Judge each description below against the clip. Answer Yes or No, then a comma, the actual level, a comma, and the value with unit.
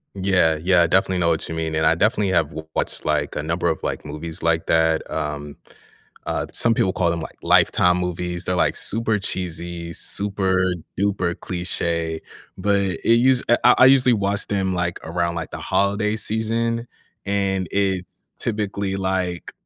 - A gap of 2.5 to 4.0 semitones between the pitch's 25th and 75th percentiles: Yes, average, 3.2 semitones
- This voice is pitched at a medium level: No, very low, 90 Hz